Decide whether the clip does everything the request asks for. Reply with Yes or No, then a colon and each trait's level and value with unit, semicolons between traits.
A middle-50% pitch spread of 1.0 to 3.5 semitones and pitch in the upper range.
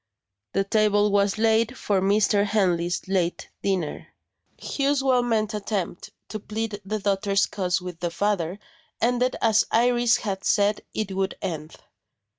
Yes: narrow, 2.4 semitones; high, 205 Hz